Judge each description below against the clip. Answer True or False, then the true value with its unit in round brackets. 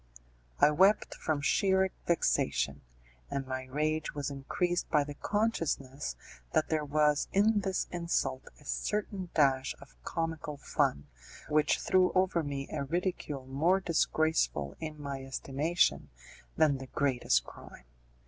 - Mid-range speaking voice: True (150 Hz)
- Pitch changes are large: False (4.2 semitones)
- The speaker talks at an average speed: False (130 wpm)